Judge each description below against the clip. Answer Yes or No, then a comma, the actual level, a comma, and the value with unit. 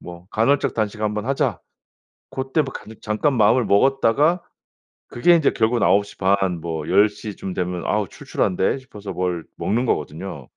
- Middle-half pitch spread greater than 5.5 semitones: No, average, 5.2 semitones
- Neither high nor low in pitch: No, low, 105 Hz